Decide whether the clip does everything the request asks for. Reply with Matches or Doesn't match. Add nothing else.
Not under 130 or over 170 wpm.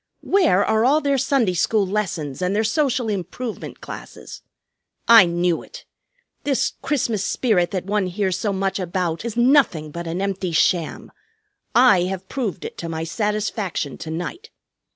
Matches